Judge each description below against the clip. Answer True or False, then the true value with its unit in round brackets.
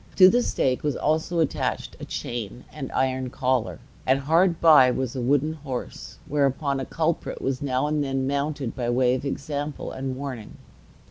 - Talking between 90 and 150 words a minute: False (175 wpm)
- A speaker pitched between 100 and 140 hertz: True (135 Hz)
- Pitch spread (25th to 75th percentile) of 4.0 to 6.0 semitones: False (2.7 semitones)